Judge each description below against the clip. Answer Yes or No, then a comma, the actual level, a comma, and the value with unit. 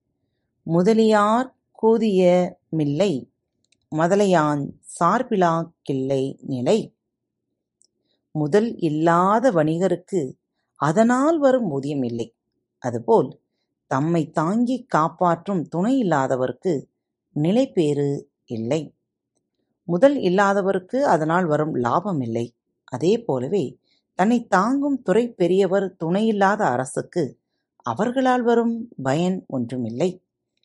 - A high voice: No, medium, 180 Hz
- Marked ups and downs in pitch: Yes, wide, 6.6 semitones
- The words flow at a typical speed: No, slow, 70 wpm